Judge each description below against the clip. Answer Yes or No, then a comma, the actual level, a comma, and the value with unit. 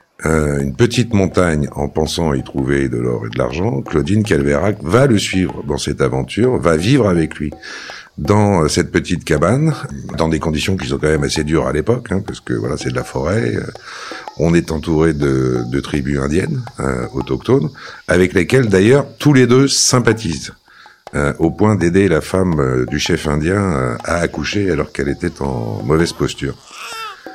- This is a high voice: No, very low, 80 Hz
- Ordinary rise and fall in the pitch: No, wide, 6.2 semitones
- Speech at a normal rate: Yes, average, 185 wpm